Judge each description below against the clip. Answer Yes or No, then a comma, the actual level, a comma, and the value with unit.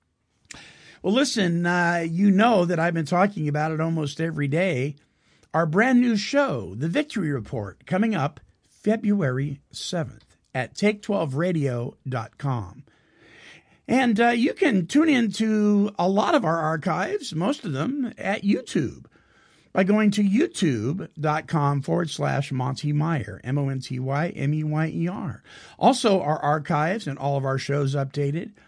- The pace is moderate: No, slow, 130 wpm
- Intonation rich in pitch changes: Yes, wide, 6.2 semitones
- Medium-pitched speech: Yes, medium, 165 Hz